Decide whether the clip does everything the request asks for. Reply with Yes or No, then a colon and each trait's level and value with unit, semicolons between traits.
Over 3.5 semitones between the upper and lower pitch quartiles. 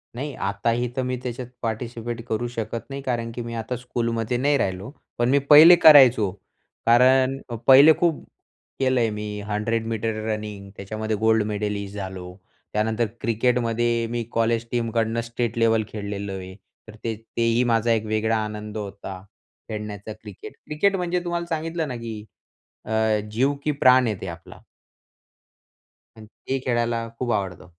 No: average, 2.8 semitones